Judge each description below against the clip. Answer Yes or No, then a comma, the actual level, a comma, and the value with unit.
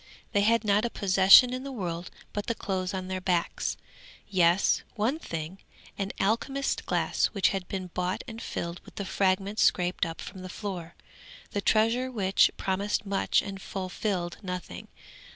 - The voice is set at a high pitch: Yes, high, 195 Hz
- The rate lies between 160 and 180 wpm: Yes, average, 165 wpm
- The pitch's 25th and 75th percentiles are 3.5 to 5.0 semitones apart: No, average, 2.7 semitones